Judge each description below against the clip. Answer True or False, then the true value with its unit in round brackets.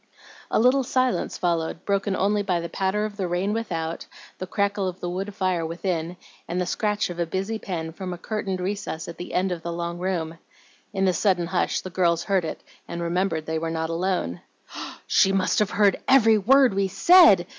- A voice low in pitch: False (185 Hz)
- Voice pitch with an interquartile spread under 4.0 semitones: True (2.9 semitones)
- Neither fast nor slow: False (210 wpm)